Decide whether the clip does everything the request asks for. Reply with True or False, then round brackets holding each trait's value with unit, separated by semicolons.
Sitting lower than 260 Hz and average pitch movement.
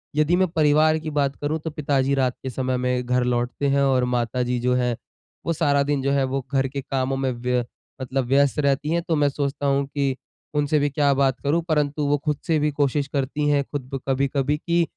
False (140 Hz; 2.1 semitones)